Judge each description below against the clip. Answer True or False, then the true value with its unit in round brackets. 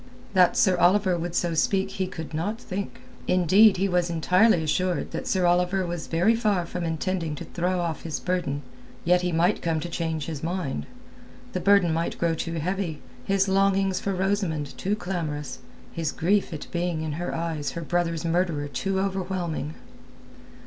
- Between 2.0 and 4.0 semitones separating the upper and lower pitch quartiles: True (2.7 semitones)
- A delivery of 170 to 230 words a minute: True (175 wpm)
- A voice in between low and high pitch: True (175 Hz)